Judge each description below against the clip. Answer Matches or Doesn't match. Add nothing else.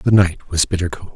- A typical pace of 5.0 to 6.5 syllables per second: Matches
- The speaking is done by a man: Matches